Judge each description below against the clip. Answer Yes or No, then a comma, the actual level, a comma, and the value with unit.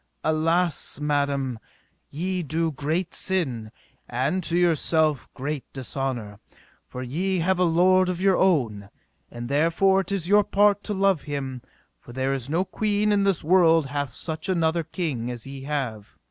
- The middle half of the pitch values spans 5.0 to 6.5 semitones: Yes, average, 5.3 semitones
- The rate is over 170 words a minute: No, average, 160 wpm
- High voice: No, medium, 160 Hz